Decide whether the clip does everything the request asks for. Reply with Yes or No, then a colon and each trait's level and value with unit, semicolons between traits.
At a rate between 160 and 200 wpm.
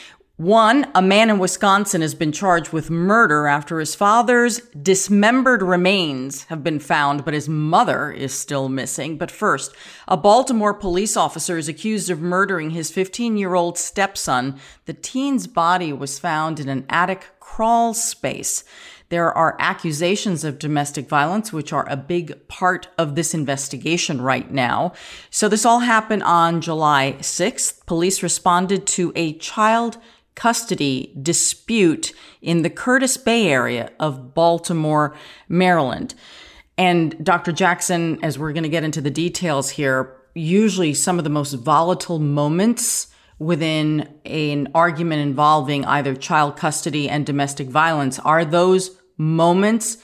No: average, 145 wpm